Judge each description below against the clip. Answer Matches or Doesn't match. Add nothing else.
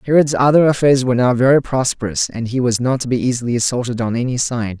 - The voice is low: Matches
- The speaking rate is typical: Doesn't match